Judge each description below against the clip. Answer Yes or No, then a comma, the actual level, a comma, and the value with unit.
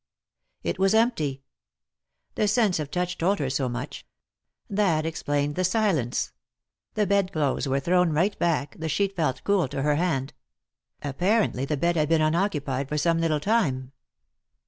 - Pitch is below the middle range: No, medium, 160 Hz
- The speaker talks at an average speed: Yes, average, 160 wpm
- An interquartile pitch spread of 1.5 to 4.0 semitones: No, average, 5.2 semitones